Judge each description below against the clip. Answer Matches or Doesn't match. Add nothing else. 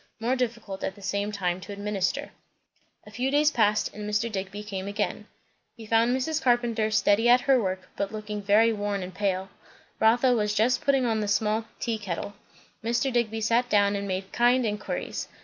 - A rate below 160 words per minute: Doesn't match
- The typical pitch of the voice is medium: Doesn't match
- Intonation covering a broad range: Doesn't match